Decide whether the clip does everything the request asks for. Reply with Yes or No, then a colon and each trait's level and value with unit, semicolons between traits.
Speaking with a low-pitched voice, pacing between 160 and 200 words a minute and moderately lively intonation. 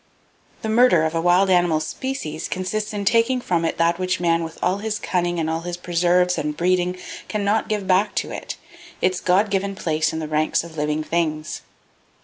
No: medium, 180 Hz; average, 195 wpm; average, 3.5 semitones